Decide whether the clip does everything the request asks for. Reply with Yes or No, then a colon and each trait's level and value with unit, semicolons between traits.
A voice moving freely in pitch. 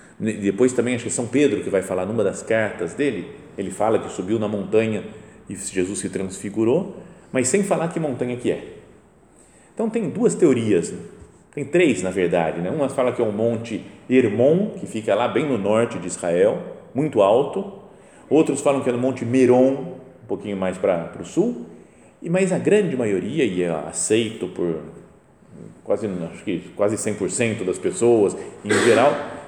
Yes: wide, 5.9 semitones